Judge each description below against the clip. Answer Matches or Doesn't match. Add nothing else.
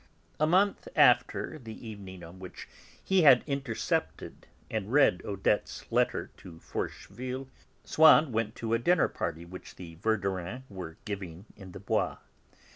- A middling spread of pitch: Doesn't match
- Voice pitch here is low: Matches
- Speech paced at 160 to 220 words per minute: Doesn't match